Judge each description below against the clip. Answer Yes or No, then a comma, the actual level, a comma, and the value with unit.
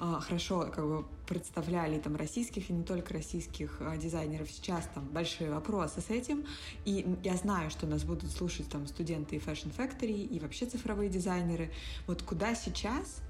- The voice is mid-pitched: Yes, medium, 175 Hz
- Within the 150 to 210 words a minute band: Yes, fast, 160 wpm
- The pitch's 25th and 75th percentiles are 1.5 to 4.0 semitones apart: No, average, 4.5 semitones